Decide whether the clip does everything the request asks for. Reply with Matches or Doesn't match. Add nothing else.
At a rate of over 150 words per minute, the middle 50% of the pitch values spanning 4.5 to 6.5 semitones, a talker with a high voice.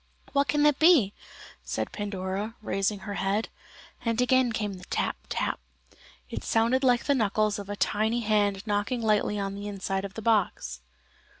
Doesn't match